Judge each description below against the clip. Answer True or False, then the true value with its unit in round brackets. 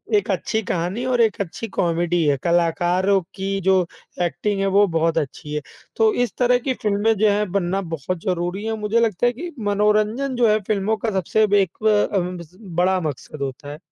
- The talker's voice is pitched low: False (195 Hz)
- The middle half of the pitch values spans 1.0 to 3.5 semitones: False (3.9 semitones)